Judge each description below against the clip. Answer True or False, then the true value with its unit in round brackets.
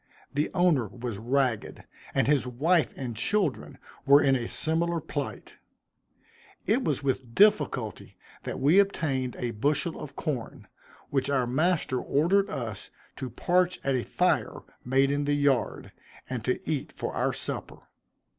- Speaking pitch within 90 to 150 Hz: True (140 Hz)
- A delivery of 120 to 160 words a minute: True (145 wpm)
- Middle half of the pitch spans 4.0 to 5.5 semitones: True (4.4 semitones)